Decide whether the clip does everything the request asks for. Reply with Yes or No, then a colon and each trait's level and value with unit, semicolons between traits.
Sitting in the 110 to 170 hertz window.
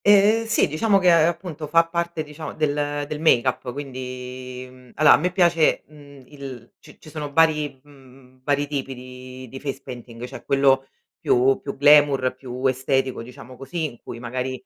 Yes: medium, 140 Hz